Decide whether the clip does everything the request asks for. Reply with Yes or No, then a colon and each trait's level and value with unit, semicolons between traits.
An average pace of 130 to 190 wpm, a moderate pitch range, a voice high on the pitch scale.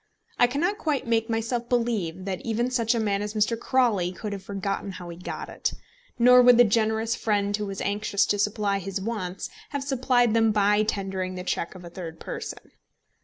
No: average, 200 wpm; average, 3.2 semitones; high, 210 Hz